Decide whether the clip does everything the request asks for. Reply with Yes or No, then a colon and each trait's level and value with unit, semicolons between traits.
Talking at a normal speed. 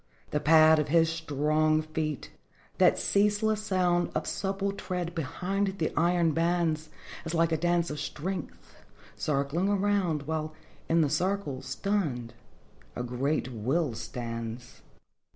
No: slow, 130 wpm